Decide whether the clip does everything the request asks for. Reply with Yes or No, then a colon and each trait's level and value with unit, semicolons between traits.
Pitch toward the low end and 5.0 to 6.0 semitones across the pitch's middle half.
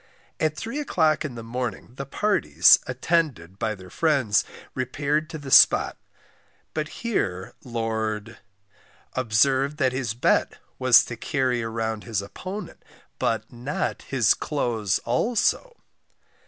Yes: low, 125 Hz; average, 5.3 semitones